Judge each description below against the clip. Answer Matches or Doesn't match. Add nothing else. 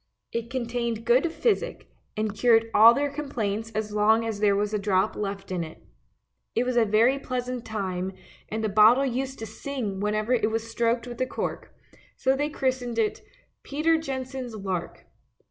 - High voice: Matches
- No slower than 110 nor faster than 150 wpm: Doesn't match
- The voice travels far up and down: Doesn't match